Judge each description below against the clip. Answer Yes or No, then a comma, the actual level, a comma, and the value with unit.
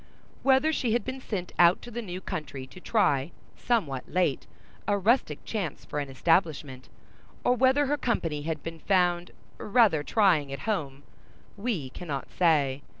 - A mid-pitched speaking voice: Yes, medium, 175 Hz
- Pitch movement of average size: No, wide, 7.5 semitones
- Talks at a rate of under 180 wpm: Yes, average, 155 wpm